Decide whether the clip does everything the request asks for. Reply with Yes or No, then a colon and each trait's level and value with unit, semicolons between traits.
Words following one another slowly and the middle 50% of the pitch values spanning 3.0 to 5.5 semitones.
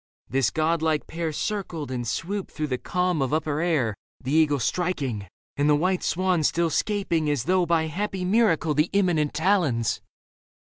No: average, 170 wpm; average, 3.7 semitones